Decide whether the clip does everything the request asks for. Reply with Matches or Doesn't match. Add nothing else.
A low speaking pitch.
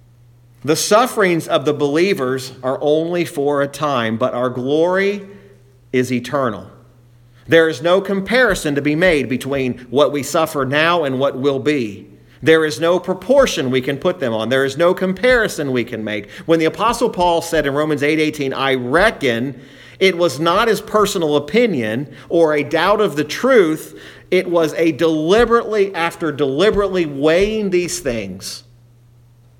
Doesn't match